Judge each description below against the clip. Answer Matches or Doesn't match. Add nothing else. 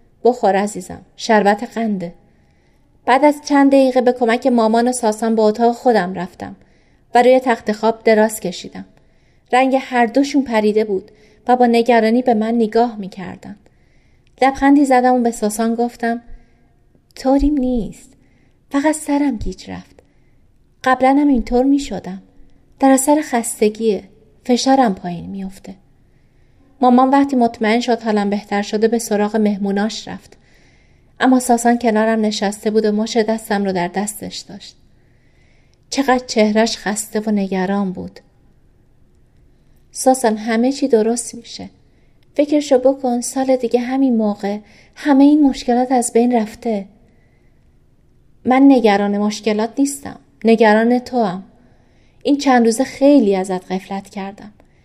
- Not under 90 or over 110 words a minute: Doesn't match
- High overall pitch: Matches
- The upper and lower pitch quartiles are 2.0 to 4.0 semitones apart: Matches